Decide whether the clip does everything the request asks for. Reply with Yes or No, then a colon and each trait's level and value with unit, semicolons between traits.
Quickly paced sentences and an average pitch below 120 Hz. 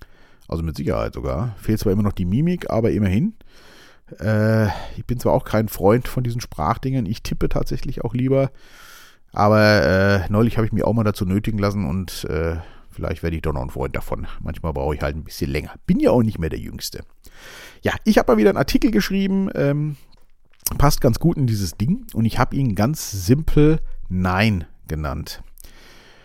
Yes: fast, 195 wpm; low, 110 Hz